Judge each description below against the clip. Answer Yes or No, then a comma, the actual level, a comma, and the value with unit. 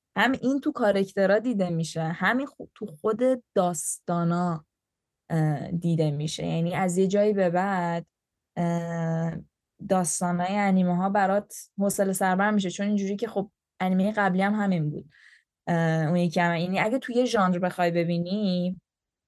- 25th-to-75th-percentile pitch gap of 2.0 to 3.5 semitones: Yes, average, 2.9 semitones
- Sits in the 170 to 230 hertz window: Yes, medium, 185 Hz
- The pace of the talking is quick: No, average, 135 wpm